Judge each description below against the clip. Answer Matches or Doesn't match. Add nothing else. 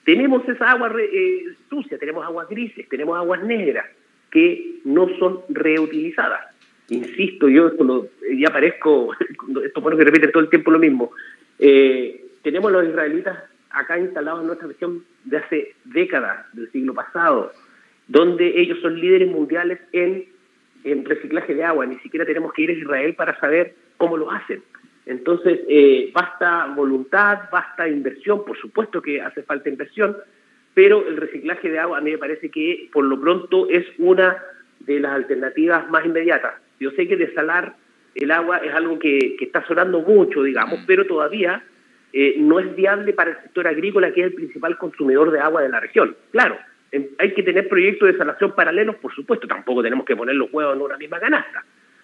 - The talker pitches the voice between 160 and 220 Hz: Matches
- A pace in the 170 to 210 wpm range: Matches